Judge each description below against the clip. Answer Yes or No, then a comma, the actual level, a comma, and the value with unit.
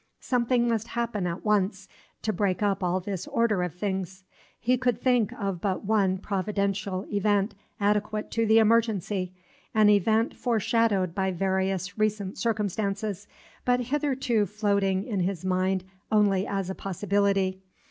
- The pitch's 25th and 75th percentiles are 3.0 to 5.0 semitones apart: No, narrow, 2.5 semitones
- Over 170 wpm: No, average, 140 wpm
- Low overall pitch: No, high, 205 Hz